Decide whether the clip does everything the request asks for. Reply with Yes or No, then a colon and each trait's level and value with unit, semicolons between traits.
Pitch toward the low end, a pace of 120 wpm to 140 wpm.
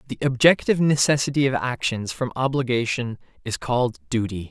Yes: low, 125 Hz; slow, 135 wpm